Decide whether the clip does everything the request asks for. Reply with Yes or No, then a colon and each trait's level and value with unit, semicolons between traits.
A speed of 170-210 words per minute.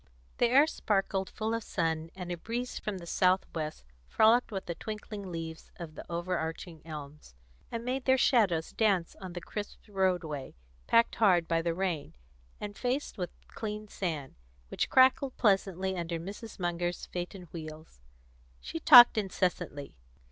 No: average, 155 wpm